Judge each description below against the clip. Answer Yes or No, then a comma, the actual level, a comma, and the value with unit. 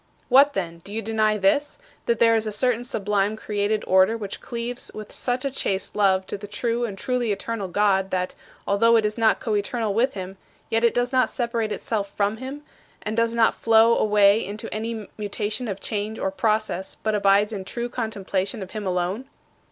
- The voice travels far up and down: No, narrow, 2.6 semitones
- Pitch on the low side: No, high, 215 Hz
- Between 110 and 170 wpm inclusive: No, average, 195 wpm